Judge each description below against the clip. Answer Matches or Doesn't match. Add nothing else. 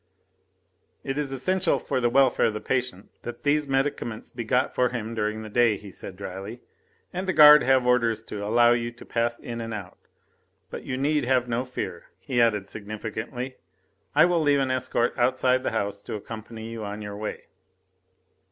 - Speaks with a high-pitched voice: Doesn't match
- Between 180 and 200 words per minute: Matches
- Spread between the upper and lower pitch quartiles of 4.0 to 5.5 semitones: Doesn't match